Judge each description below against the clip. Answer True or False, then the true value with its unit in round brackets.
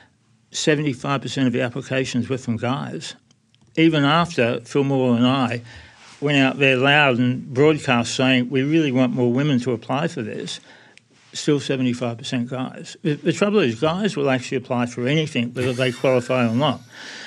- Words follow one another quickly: False (160 wpm)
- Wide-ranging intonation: False (2.5 semitones)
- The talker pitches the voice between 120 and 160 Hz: True (130 Hz)